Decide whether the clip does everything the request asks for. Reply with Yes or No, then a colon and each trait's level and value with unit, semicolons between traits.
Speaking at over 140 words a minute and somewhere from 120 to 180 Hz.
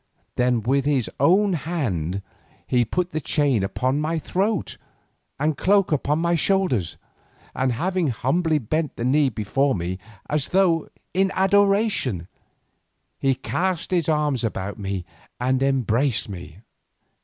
No: slow, 135 wpm; medium, 140 Hz